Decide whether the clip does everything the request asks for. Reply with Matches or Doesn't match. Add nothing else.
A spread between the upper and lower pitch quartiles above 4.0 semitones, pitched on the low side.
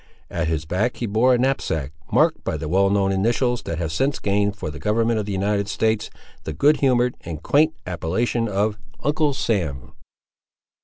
Matches